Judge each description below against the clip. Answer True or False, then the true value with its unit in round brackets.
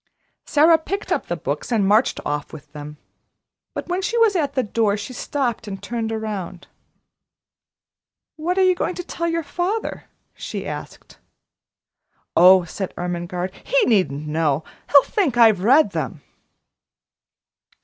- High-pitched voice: True (225 Hz)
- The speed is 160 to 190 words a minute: False (145 wpm)